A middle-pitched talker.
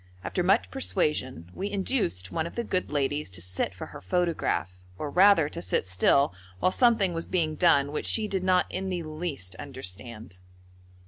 Yes: medium, 150 Hz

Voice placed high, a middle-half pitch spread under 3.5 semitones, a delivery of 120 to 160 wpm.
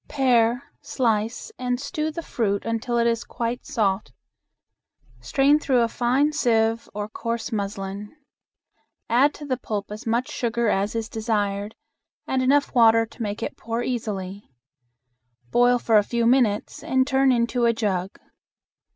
Yes: high, 230 Hz; average, 2.9 semitones; average, 150 wpm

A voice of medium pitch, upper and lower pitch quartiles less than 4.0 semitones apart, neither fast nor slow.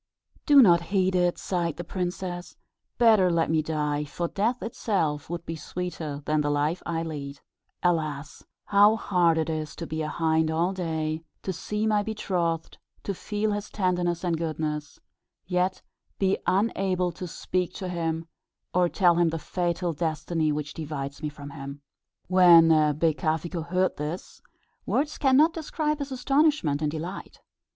Yes: medium, 170 Hz; average, 3.2 semitones; average, 160 wpm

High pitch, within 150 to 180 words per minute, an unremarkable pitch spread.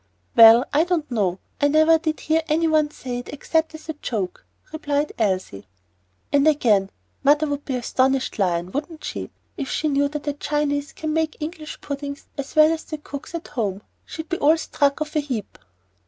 No: very high, 290 Hz; average, 190 wpm; average, 3.4 semitones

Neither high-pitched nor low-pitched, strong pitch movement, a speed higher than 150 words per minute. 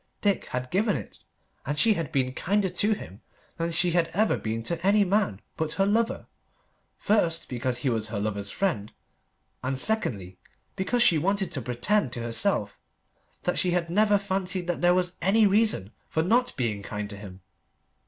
Yes: medium, 170 Hz; wide, 8.9 semitones; average, 180 wpm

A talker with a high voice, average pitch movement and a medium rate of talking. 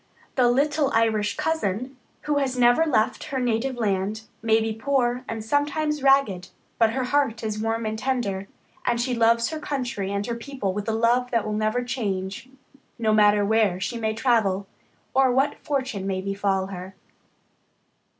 Yes: high, 230 Hz; average, 3.9 semitones; average, 170 wpm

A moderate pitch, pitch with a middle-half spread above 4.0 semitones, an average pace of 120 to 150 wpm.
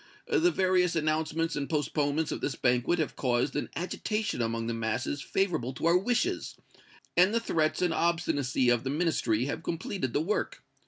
No: medium, 155 Hz; wide, 5.5 semitones; average, 170 wpm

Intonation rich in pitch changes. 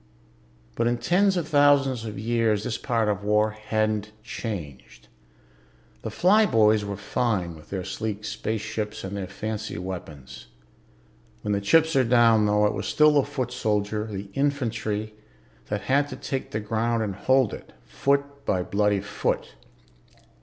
No: average, 3.7 semitones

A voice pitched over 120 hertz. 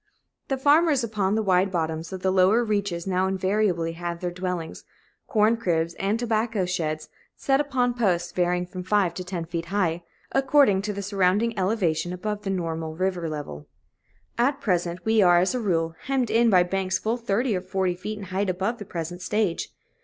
Yes: high, 190 Hz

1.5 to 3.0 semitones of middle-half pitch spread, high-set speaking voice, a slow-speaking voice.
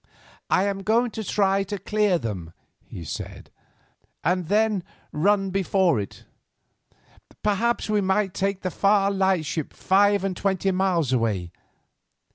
Yes: average, 2.7 semitones; high, 195 Hz; slow, 130 wpm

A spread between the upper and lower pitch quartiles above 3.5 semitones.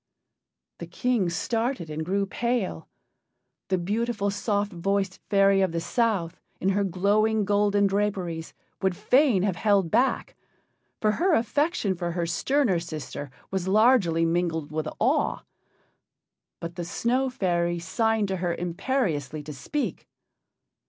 Yes: average, 4.5 semitones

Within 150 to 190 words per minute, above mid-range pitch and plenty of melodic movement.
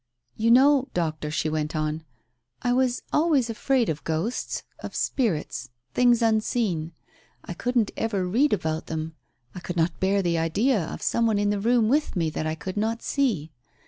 Yes: average, 185 wpm; high, 205 Hz; wide, 7.0 semitones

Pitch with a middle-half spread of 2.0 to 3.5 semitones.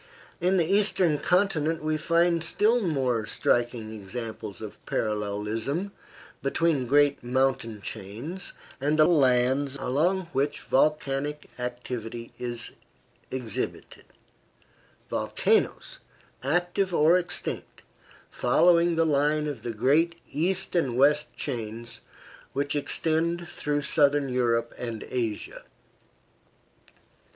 No: wide, 5.5 semitones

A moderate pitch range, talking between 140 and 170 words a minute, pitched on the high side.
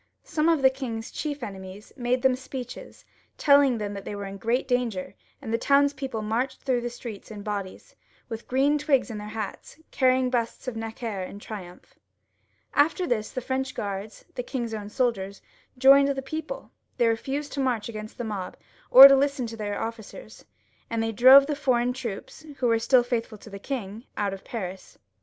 No: average, 3.9 semitones; average, 185 wpm; high, 240 Hz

